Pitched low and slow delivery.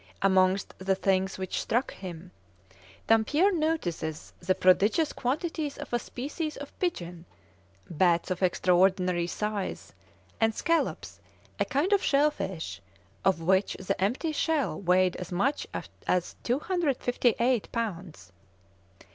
No: high, 195 Hz; slow, 120 wpm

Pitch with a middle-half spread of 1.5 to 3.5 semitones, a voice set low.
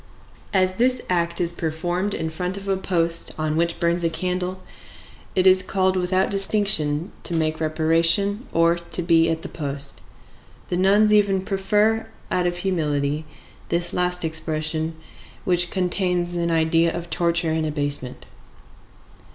No: narrow, 2.6 semitones; medium, 175 Hz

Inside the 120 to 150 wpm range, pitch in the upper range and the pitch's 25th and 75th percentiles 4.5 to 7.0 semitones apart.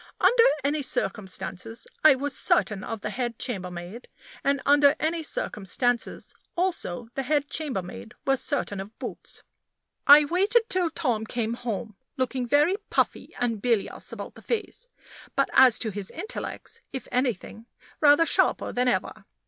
Yes: average, 145 wpm; very high, 250 Hz; average, 5.1 semitones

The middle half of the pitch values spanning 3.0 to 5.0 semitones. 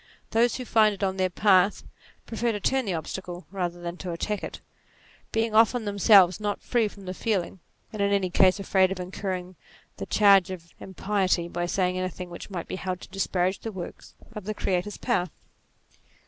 No: narrow, 2.4 semitones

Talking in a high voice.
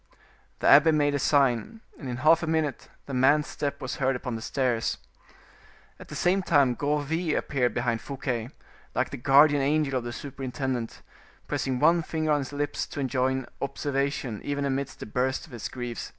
No: medium, 140 Hz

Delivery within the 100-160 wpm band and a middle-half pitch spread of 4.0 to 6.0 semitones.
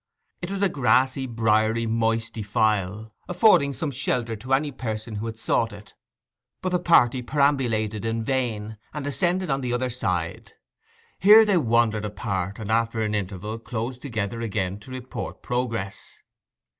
No: average, 155 wpm; average, 3.6 semitones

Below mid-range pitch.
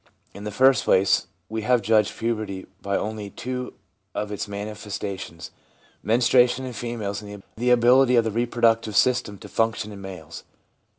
Yes: low, 110 Hz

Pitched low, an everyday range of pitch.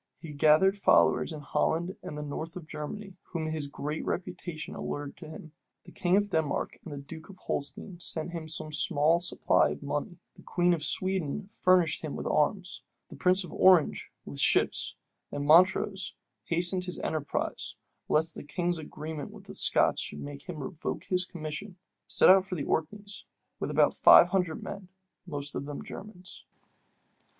No: medium, 165 Hz; average, 3.4 semitones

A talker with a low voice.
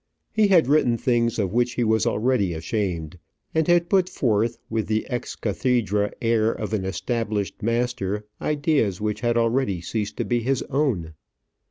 Yes: low, 115 Hz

